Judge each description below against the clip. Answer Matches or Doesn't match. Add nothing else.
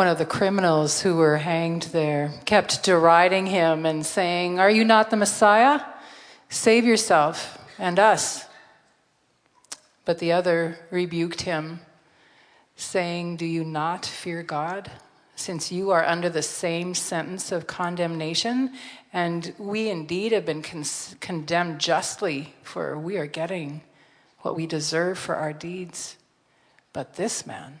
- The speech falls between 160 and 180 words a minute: Doesn't match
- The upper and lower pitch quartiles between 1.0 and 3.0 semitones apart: Matches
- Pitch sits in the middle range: Matches